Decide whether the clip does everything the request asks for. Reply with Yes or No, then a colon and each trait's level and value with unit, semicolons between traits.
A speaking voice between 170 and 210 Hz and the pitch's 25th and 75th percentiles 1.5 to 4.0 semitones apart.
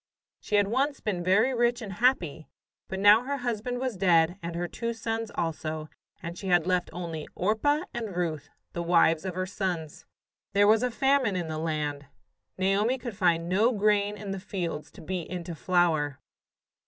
No: high, 190 Hz; average, 4.9 semitones